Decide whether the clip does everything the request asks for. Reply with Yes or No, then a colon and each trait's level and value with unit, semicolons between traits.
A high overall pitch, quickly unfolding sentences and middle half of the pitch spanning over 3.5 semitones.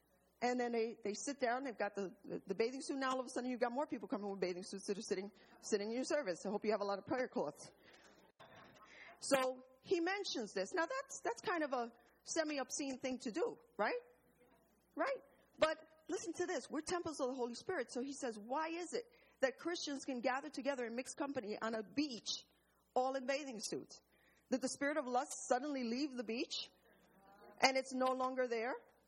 Yes: very high, 260 Hz; fast, 215 wpm; average, 3.9 semitones